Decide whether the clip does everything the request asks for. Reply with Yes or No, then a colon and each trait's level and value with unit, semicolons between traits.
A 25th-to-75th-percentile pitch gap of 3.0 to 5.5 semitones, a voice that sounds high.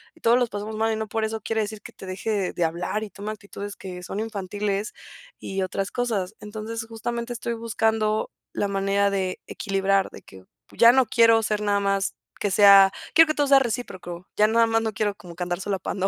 No: narrow, 2.4 semitones; high, 210 Hz